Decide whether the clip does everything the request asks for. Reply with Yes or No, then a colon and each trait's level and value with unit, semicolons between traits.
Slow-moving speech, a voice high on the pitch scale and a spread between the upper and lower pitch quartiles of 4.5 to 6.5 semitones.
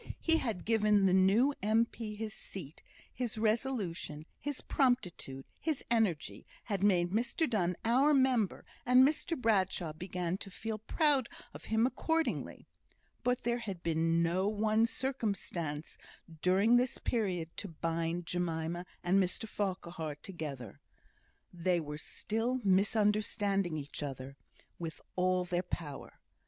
Yes: slow, 130 wpm; high, 195 Hz; average, 5.1 semitones